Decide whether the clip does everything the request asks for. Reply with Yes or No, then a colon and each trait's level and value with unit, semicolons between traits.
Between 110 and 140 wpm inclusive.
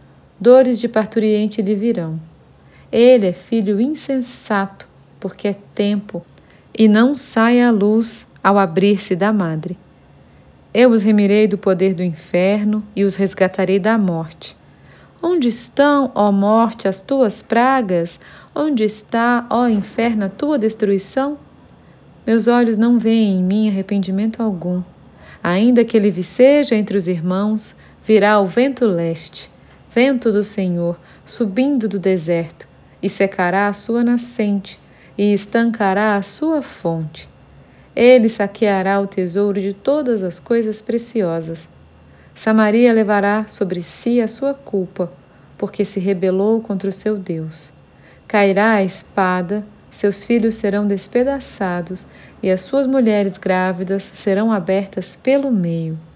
Yes: average, 130 wpm